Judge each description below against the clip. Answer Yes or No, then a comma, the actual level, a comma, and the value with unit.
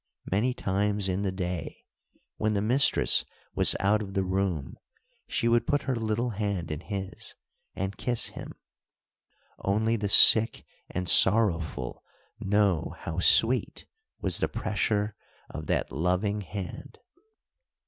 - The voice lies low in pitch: Yes, low, 100 Hz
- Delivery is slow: Yes, slow, 130 wpm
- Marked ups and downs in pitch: No, average, 2.8 semitones